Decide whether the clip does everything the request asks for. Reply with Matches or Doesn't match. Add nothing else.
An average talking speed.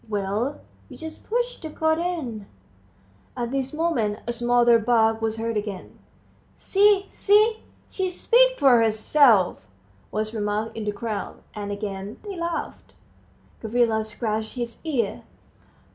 Doesn't match